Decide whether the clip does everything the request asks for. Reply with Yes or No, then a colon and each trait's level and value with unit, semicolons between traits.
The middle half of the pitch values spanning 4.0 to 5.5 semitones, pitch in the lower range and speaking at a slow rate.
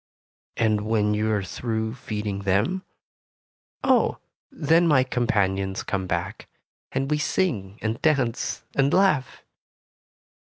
Yes: average, 5.2 semitones; low, 115 Hz; slow, 115 wpm